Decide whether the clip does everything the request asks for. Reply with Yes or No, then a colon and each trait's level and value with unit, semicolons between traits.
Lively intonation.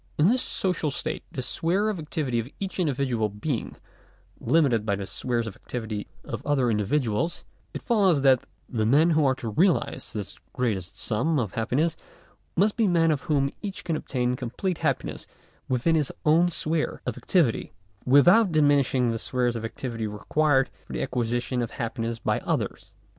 Yes: wide, 5.7 semitones